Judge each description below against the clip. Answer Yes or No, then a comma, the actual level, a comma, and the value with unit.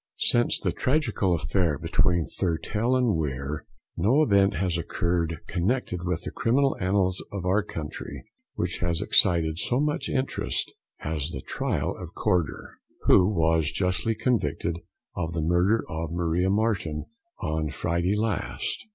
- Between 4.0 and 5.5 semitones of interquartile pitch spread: Yes, average, 4.5 semitones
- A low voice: Yes, very low, 90 Hz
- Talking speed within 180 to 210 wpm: No, average, 140 wpm